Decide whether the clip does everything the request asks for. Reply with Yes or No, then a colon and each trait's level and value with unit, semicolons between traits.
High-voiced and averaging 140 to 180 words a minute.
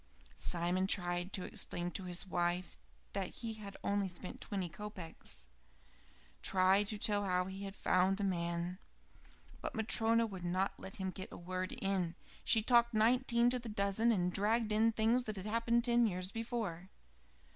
Yes: high, 195 Hz; average, 165 wpm